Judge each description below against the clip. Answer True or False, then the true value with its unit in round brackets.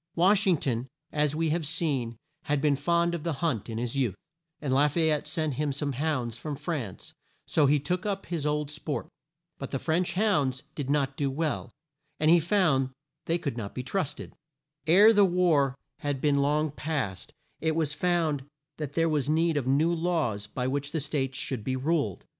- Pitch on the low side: False (150 Hz)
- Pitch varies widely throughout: False (3.5 semitones)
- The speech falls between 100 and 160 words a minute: False (195 wpm)